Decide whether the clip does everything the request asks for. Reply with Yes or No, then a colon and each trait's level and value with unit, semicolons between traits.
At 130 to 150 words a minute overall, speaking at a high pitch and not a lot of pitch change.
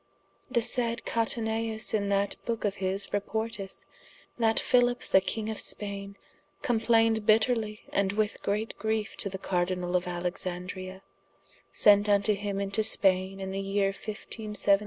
Yes: average, 140 wpm; high, 205 Hz; narrow, 2.3 semitones